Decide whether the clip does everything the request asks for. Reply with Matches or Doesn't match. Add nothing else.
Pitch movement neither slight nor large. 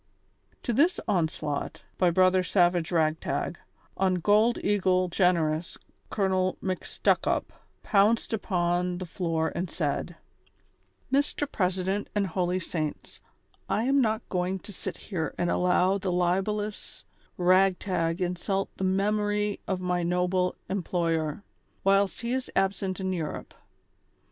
Doesn't match